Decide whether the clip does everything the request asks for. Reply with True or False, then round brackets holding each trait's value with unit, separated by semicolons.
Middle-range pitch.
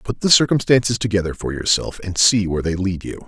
False (100 Hz)